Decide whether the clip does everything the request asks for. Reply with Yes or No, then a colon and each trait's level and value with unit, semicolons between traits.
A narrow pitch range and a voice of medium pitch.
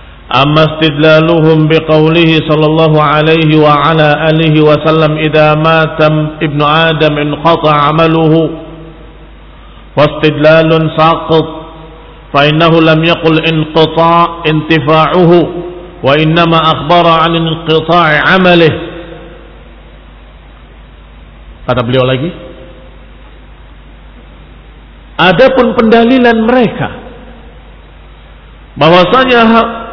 Yes: narrow, 1.8 semitones; medium, 160 Hz